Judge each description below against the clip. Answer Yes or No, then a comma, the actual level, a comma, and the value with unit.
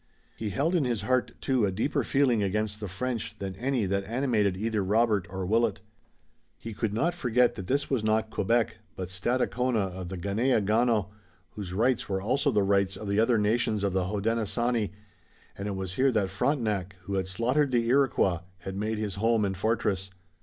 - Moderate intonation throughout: Yes, average, 3.6 semitones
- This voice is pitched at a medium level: No, low, 110 Hz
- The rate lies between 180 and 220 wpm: Yes, average, 190 wpm